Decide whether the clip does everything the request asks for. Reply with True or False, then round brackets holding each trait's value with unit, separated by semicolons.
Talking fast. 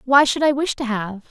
True (275 wpm)